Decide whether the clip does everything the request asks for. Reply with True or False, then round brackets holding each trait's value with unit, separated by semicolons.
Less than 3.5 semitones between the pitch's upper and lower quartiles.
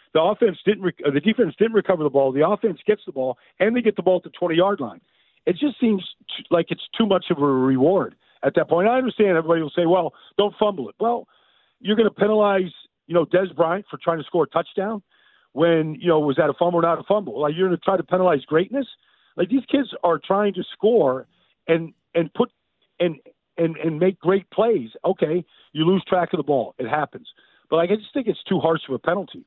False (4.1 semitones)